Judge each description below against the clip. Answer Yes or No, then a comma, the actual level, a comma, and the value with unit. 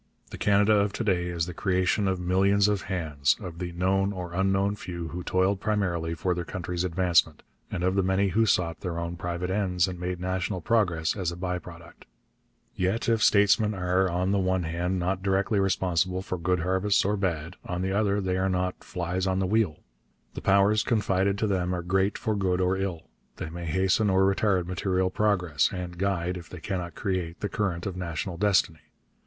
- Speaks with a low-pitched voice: Yes, very low, 95 Hz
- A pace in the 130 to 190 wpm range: No, average, 200 wpm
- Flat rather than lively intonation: Yes, narrow, 1.9 semitones